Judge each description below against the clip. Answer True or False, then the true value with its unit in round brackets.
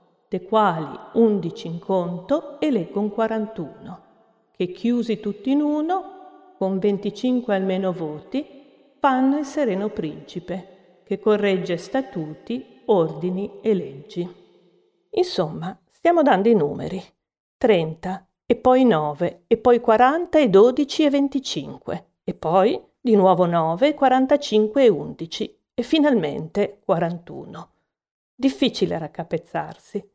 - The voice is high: True (210 Hz)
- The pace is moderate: False (110 wpm)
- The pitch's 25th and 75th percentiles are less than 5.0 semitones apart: False (6.7 semitones)